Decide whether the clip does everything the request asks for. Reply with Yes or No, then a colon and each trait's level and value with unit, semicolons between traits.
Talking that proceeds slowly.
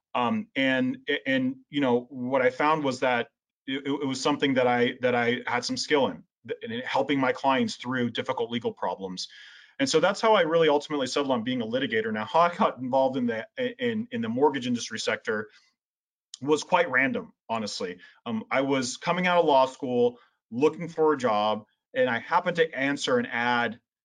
No: average, 195 wpm